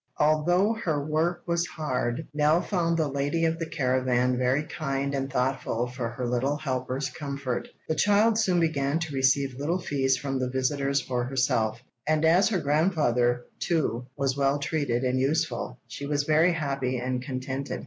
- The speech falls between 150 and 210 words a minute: Yes, average, 170 wpm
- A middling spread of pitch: Yes, average, 3.6 semitones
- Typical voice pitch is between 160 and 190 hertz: No, medium, 140 Hz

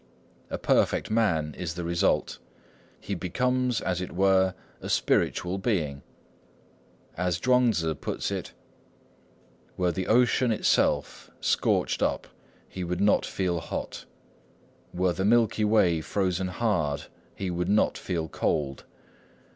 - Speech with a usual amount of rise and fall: Yes, average, 3.7 semitones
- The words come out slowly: Yes, slow, 125 wpm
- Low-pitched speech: Yes, very low, 90 Hz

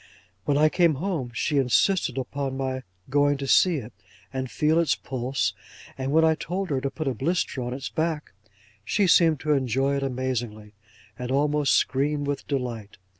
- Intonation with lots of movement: No, average, 3.0 semitones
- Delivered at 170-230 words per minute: Yes, average, 175 wpm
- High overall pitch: No, medium, 140 Hz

